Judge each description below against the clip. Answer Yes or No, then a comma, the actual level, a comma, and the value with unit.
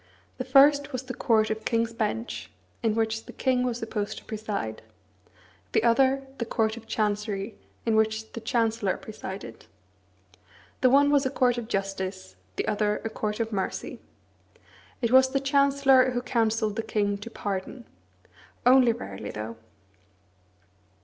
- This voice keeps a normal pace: Yes, average, 150 wpm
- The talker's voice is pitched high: Yes, high, 225 Hz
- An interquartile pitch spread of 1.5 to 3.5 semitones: Yes, average, 3.2 semitones